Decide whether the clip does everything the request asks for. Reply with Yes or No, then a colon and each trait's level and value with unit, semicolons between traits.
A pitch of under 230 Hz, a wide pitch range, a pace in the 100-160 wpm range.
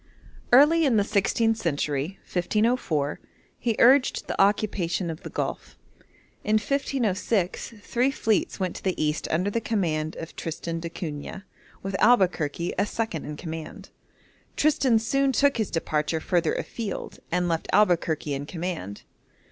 Yes: high, 190 Hz; wide, 5.7 semitones; average, 140 wpm